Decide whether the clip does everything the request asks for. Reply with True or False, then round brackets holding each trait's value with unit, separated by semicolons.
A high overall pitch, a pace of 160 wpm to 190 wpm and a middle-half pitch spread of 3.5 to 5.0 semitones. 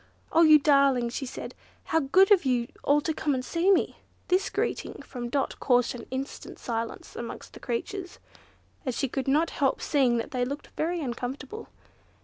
True (275 Hz; 180 wpm; 4.4 semitones)